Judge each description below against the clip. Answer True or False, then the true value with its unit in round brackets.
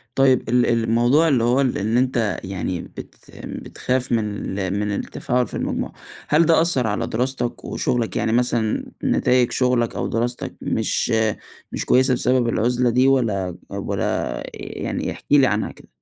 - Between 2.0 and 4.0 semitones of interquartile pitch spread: True (2.5 semitones)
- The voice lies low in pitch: True (120 Hz)